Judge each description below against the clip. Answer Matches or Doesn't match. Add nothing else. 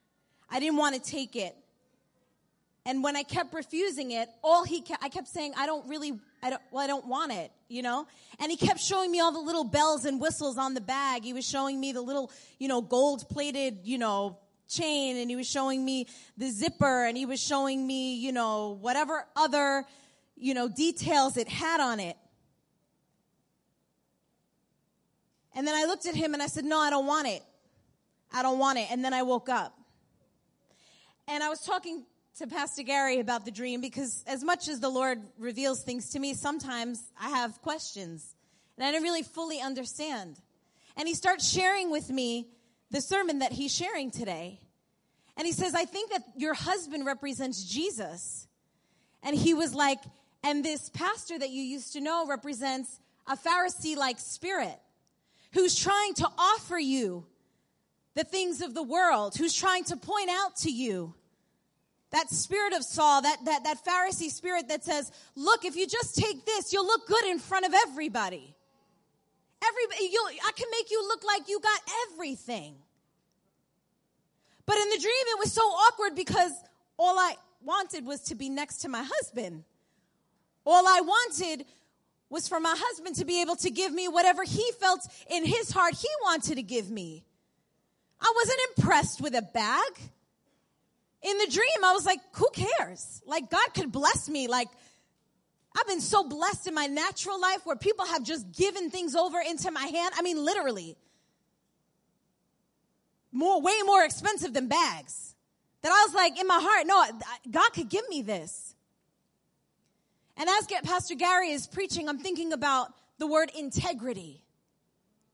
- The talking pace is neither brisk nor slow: Matches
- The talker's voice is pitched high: Matches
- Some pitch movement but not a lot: Doesn't match